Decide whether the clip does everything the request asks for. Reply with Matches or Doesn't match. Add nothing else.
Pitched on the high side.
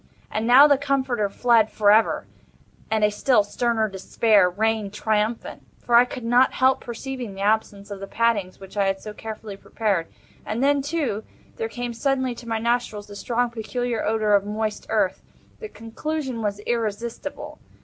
Matches